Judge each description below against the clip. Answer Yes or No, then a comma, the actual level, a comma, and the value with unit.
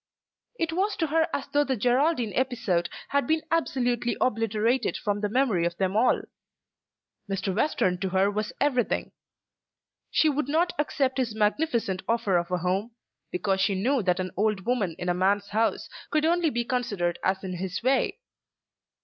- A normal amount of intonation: No, wide, 6.1 semitones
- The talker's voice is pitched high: Yes, high, 225 Hz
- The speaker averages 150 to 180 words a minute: Yes, average, 170 wpm